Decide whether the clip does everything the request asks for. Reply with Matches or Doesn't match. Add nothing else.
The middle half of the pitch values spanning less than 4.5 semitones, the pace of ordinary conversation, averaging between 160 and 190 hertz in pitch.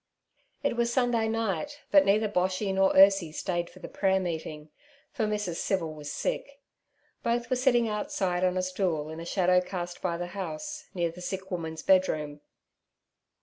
Matches